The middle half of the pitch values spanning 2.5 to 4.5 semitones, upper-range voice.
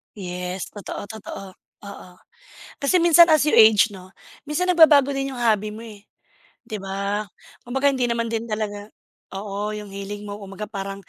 Yes: average, 3.9 semitones; high, 210 Hz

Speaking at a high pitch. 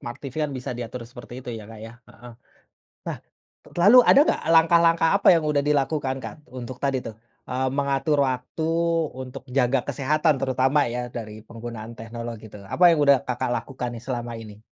No: low, 130 Hz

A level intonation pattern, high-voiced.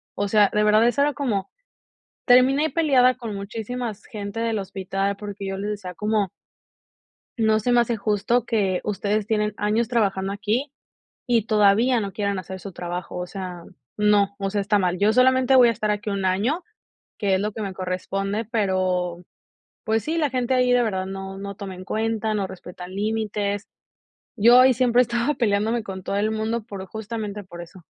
No: average, 3.0 semitones; high, 210 Hz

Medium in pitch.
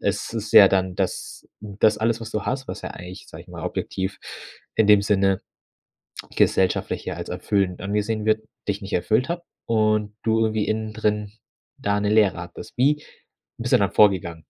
No: low, 105 Hz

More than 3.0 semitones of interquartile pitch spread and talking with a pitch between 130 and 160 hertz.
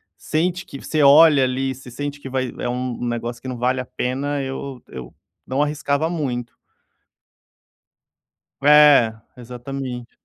No: average, 2.7 semitones; low, 135 Hz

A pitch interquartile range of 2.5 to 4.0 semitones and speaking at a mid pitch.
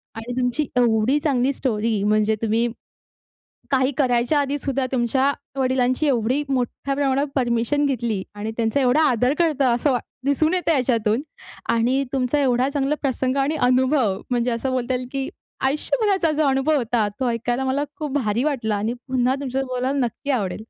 No: average, 2.8 semitones; very high, 255 Hz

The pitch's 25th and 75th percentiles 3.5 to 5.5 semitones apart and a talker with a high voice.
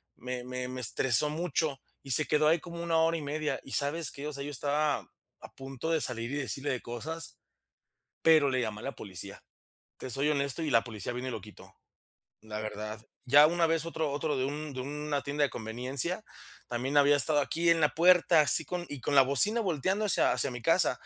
No: average, 4.0 semitones; medium, 145 Hz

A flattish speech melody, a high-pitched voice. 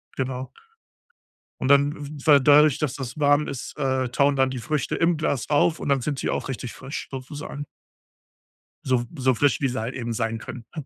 No: narrow, 2.2 semitones; low, 135 Hz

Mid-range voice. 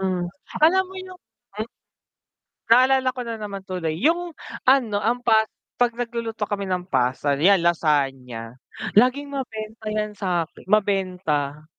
No: high, 210 Hz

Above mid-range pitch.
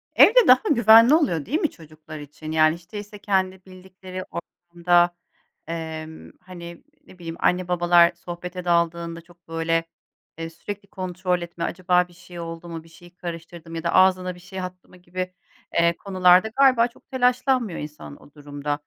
No: medium, 175 Hz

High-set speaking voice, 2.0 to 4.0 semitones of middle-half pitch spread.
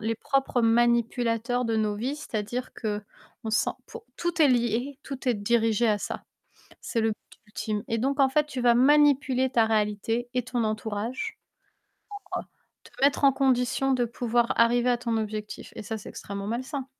Yes: high, 240 Hz; average, 2.9 semitones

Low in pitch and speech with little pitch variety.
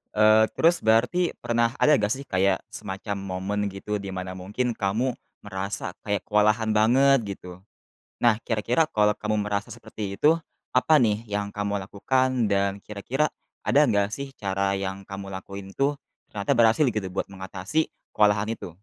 No: low, 105 Hz; average, 3.2 semitones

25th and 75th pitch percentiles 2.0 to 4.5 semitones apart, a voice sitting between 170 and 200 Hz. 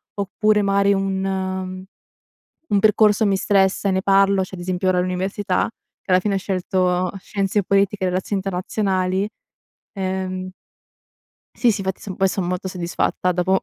No: narrow, 1.2 semitones; high, 190 Hz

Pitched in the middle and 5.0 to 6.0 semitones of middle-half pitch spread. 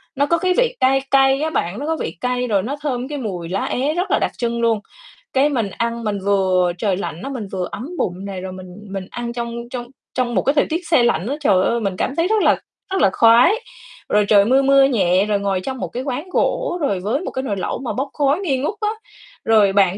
No: high, 240 Hz; wide, 5.6 semitones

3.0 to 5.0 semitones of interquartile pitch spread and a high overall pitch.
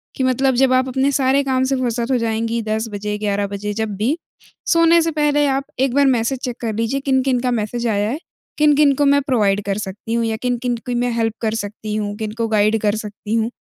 Yes: average, 3.7 semitones; high, 235 Hz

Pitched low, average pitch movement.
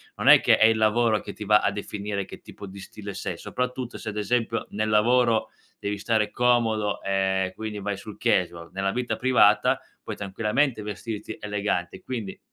No: low, 105 Hz; narrow, 2.3 semitones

